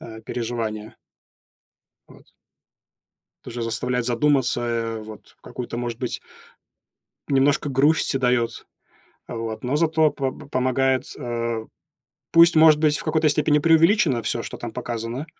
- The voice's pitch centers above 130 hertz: No, low, 125 Hz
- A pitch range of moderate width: Yes, average, 4.2 semitones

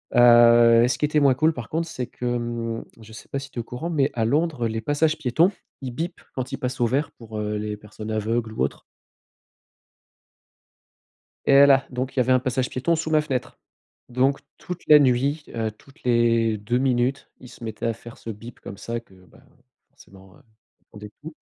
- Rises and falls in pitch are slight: No, average, 3.4 semitones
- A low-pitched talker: Yes, low, 125 Hz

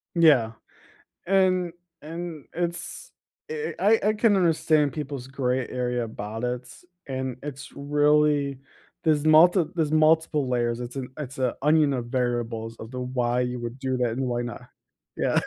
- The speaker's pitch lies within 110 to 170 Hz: Yes, low, 135 Hz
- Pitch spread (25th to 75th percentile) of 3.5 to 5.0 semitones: Yes, average, 4.2 semitones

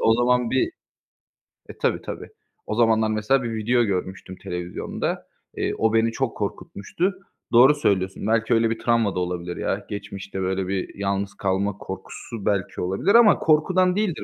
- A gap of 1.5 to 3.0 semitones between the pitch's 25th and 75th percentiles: No, average, 4.1 semitones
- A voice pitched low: Yes, low, 110 Hz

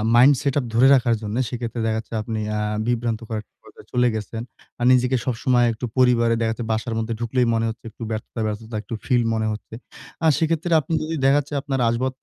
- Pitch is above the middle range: No, low, 120 Hz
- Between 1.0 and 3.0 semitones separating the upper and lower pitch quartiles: Yes, narrow, 2.4 semitones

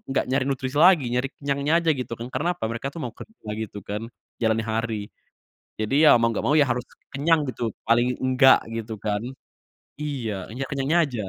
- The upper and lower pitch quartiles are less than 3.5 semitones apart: No, average, 3.8 semitones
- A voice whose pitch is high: No, low, 125 Hz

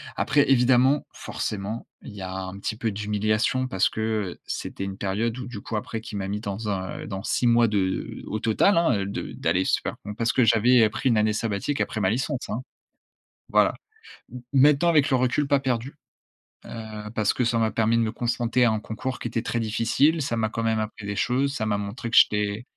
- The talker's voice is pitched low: Yes, low, 115 Hz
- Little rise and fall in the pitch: No, average, 3.2 semitones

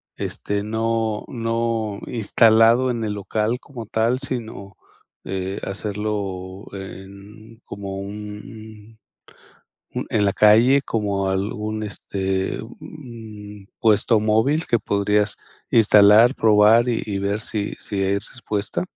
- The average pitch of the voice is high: No, low, 105 Hz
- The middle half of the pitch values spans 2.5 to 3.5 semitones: No, narrow, 2.1 semitones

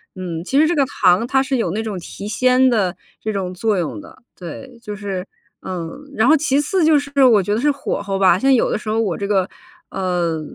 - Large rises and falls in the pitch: Yes, wide, 6.3 semitones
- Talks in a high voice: Yes, high, 215 Hz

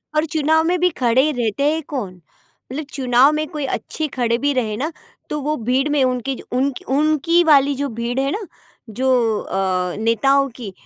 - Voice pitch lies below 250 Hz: No, very high, 270 Hz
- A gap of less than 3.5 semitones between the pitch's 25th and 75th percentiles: No, average, 3.9 semitones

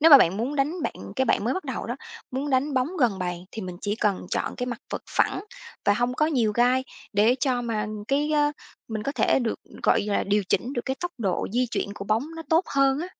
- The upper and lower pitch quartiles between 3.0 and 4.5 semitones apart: No, average, 4.9 semitones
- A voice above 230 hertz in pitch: Yes, very high, 250 Hz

